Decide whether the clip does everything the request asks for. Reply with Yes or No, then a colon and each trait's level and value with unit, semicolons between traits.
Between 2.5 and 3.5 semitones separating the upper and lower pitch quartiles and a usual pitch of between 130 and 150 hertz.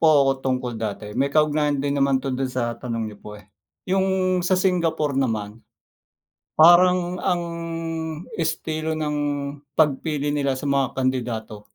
No: average, 4.2 semitones; medium, 140 Hz